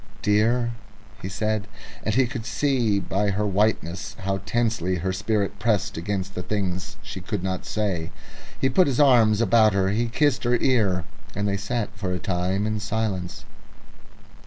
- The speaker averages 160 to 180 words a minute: Yes, average, 165 wpm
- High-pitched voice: No, low, 105 Hz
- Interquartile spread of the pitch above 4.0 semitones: No, average, 3.1 semitones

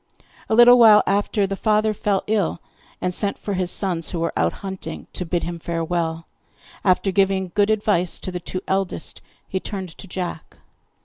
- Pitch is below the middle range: No, high, 190 Hz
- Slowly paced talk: No, average, 180 wpm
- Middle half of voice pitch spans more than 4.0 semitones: No, average, 2.7 semitones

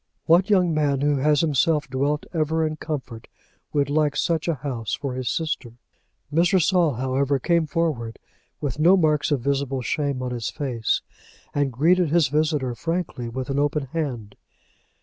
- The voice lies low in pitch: No, medium, 145 Hz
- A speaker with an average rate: Yes, average, 165 wpm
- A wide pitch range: No, average, 3.5 semitones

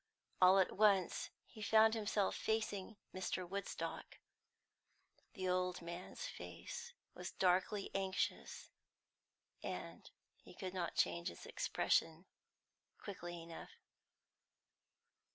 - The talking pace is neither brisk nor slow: No, slow, 100 wpm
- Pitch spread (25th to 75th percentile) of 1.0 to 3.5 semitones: Yes, narrow, 2.6 semitones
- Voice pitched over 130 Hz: Yes, high, 190 Hz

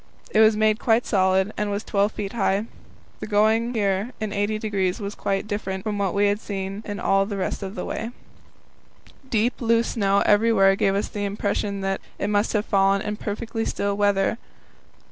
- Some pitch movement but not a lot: No, narrow, 1.7 semitones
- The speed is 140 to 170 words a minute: No, average, 185 wpm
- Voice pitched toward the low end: No, high, 205 Hz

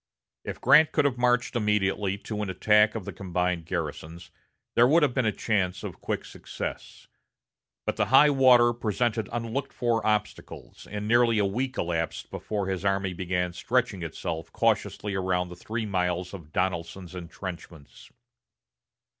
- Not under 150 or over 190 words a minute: Yes, average, 155 wpm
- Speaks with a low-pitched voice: Yes, low, 100 Hz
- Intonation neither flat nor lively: Yes, average, 4.7 semitones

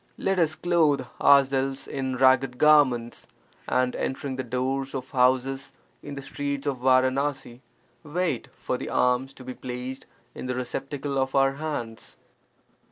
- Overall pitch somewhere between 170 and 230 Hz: No, low, 135 Hz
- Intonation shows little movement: Yes, narrow, 1.7 semitones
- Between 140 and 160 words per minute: Yes, average, 145 wpm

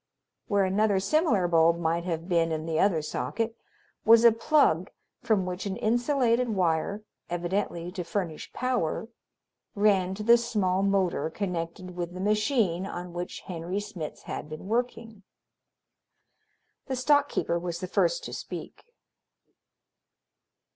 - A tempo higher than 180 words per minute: No, slow, 135 wpm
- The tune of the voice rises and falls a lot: No, average, 4.7 semitones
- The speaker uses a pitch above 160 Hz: Yes, high, 190 Hz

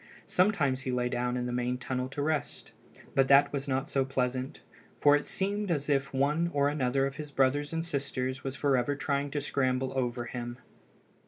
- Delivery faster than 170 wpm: Yes, average, 190 wpm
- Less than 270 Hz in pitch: Yes, low, 135 Hz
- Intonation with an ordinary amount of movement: No, narrow, 2.2 semitones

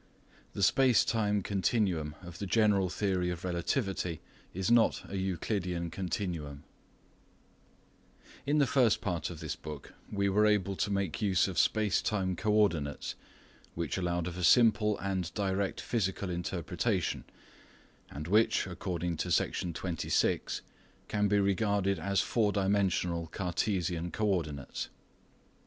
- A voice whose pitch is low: Yes, very low, 95 Hz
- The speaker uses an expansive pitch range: No, average, 3.0 semitones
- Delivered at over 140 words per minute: No, slow, 135 wpm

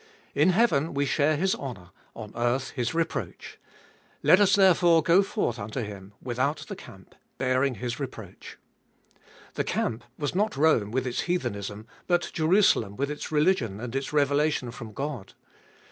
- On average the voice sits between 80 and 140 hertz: Yes, low, 135 Hz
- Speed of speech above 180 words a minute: No, average, 155 wpm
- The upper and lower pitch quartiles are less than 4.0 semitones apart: No, wide, 5.6 semitones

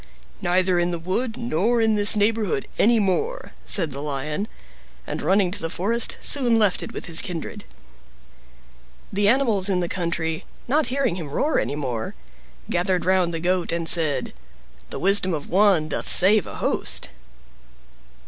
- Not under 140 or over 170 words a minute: Yes, average, 160 wpm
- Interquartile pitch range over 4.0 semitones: Yes, average, 4.4 semitones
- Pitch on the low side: No, medium, 185 Hz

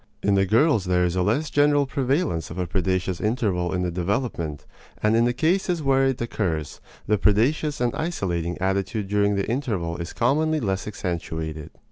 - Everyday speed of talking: Yes, average, 175 wpm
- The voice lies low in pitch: Yes, low, 100 Hz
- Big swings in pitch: Yes, wide, 6.9 semitones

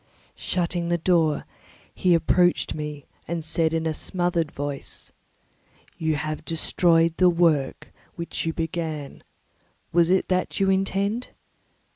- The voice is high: No, medium, 165 Hz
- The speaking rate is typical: No, slow, 130 wpm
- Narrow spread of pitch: Yes, narrow, 2.1 semitones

